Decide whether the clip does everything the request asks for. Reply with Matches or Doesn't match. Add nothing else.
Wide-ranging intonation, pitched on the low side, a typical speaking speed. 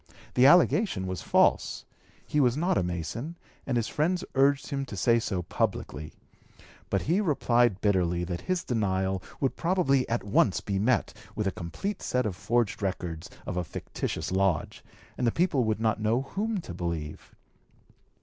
Matches